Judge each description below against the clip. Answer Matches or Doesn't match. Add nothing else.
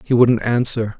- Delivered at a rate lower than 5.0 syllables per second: Matches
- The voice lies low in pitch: Matches